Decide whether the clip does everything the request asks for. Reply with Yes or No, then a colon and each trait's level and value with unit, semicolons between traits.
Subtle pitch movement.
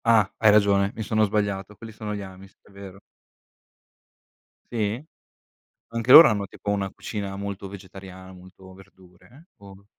Yes: narrow, 1.8 semitones